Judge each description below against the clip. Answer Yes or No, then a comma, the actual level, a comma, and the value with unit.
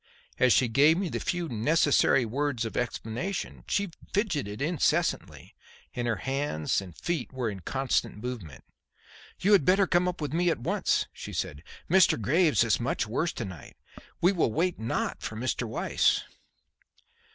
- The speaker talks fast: No, average, 165 wpm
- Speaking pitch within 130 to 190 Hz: Yes, low, 135 Hz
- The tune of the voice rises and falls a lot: Yes, wide, 7.3 semitones